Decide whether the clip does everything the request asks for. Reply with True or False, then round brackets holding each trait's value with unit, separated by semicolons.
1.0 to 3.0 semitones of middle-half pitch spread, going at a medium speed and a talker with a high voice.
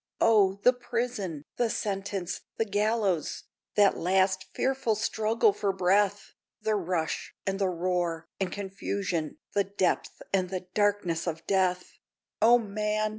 False (2.7 semitones; 130 wpm; 195 Hz)